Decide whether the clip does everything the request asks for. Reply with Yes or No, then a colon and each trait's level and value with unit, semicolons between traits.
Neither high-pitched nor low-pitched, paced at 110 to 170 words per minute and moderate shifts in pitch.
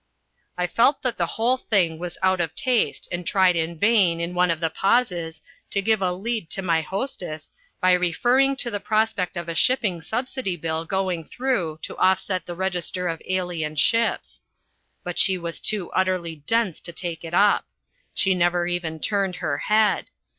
No: medium, 180 Hz; average, 180 wpm; average, 3.9 semitones